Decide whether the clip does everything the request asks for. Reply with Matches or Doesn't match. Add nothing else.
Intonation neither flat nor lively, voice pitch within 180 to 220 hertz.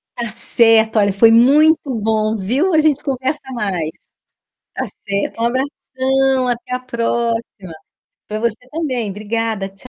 Doesn't match